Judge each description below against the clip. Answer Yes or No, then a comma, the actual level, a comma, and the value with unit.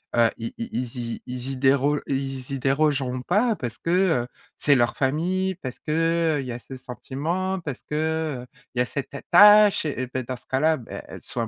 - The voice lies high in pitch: No, medium, 140 Hz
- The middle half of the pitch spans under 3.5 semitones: No, average, 4.1 semitones